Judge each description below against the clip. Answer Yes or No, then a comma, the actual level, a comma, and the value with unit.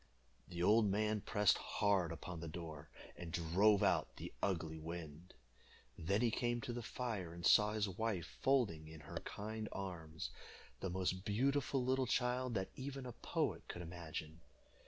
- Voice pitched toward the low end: Yes, very low, 95 Hz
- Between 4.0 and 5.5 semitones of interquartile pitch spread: Yes, average, 5.1 semitones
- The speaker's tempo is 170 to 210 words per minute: No, average, 160 wpm